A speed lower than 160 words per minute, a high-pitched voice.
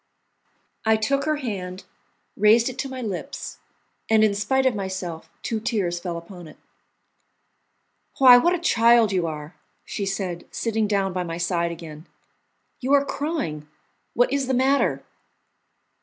Yes: average, 150 wpm; high, 215 Hz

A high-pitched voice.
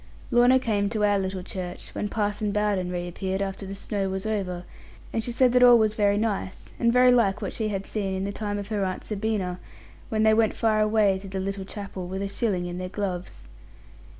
Yes: high, 200 Hz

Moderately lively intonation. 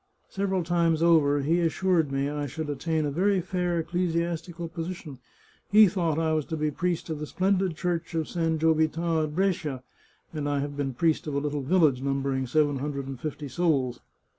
Yes: average, 3.0 semitones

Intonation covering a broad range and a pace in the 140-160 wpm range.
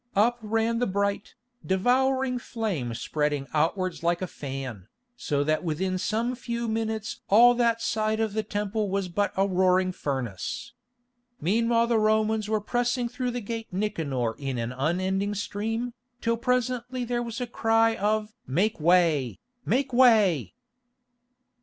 No: average, 4.7 semitones; average, 145 wpm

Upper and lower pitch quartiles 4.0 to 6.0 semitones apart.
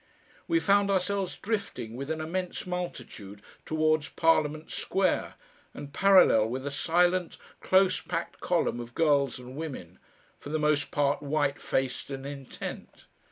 Yes: average, 4.6 semitones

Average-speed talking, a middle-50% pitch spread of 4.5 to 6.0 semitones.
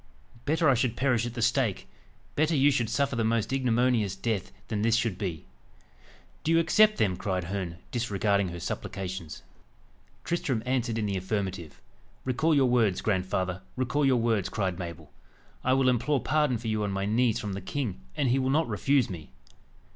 Yes: average, 180 wpm; average, 5.1 semitones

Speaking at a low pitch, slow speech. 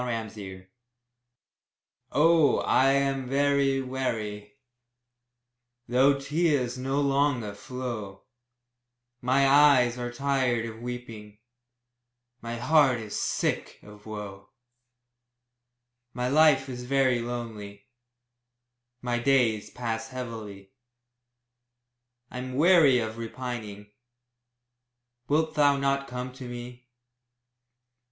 Yes: low, 125 Hz; slow, 90 wpm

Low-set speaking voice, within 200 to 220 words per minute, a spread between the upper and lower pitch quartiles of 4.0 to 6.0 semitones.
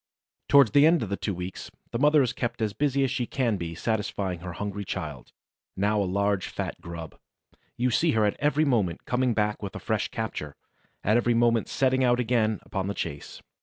Yes: low, 110 Hz; fast, 205 wpm; average, 4.5 semitones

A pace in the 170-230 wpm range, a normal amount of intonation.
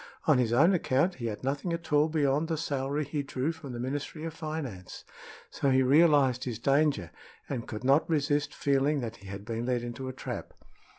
Yes: average, 200 wpm; average, 3.5 semitones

